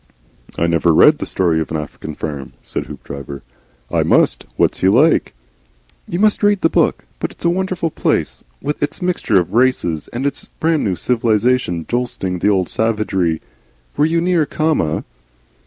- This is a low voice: Yes, low, 115 Hz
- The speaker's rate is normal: Yes, average, 170 wpm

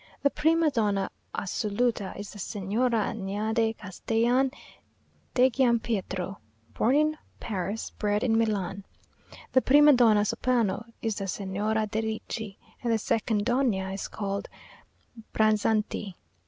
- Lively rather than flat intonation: No, average, 3.0 semitones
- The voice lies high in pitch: Yes, high, 220 Hz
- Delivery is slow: Yes, slow, 120 wpm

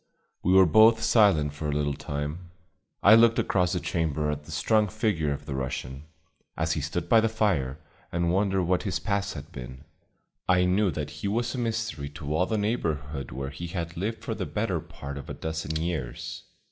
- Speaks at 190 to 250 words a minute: Yes, average, 200 wpm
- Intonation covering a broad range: Yes, wide, 5.7 semitones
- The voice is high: No, very low, 85 Hz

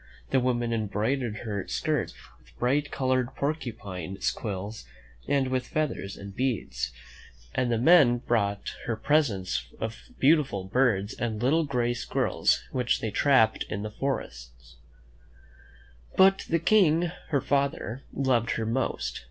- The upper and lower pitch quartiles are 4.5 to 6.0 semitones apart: Yes, average, 4.9 semitones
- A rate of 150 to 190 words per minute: No, slow, 135 wpm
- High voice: No, low, 120 Hz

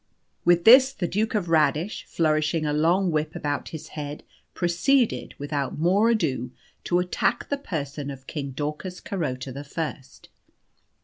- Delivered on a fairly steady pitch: No, average, 3.9 semitones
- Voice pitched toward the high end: No, medium, 160 Hz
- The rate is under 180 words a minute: Yes, average, 145 wpm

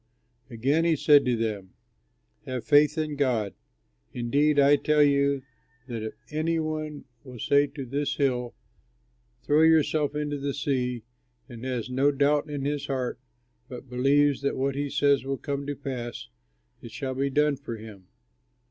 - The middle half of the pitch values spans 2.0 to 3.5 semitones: Yes, narrow, 2.6 semitones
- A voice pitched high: No, medium, 140 Hz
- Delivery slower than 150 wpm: No, average, 160 wpm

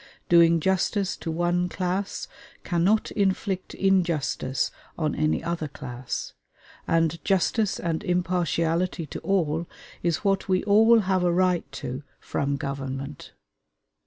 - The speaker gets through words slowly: Yes, slow, 120 wpm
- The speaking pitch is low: No, medium, 175 Hz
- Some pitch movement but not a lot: Yes, average, 3.3 semitones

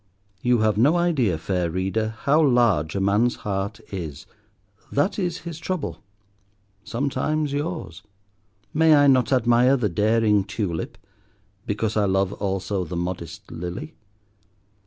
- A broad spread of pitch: Yes, wide, 6.2 semitones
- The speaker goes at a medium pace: No, slow, 125 wpm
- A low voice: Yes, low, 105 Hz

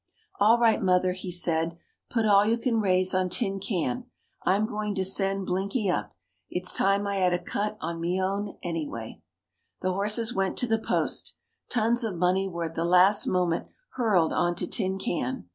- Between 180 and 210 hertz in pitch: Yes, high, 190 Hz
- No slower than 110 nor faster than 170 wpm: No, average, 185 wpm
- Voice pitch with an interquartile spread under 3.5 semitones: Yes, average, 2.9 semitones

